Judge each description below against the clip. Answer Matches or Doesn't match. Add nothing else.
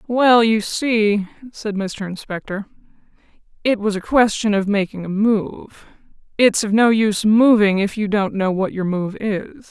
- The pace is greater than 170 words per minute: Doesn't match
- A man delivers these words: Doesn't match